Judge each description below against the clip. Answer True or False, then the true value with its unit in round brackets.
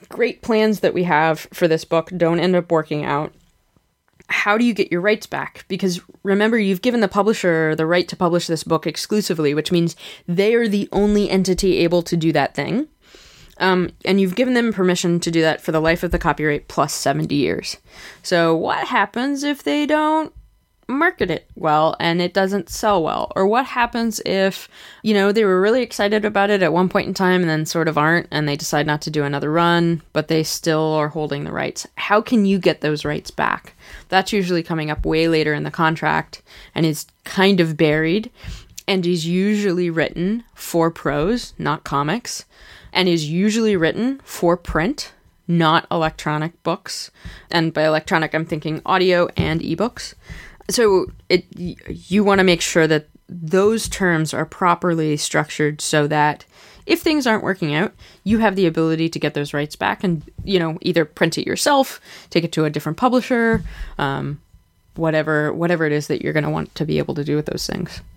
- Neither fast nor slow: True (195 wpm)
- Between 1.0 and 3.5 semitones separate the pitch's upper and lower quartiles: False (4.2 semitones)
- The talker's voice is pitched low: False (175 Hz)